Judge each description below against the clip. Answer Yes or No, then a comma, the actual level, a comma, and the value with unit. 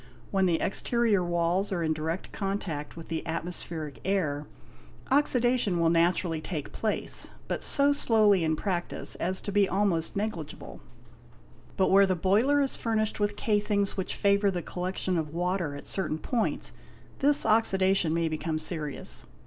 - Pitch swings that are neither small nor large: Yes, average, 3.9 semitones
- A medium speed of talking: Yes, average, 150 wpm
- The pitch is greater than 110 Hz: Yes, medium, 185 Hz